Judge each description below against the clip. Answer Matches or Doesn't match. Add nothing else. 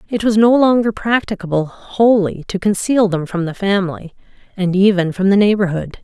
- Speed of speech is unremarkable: Matches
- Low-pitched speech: Doesn't match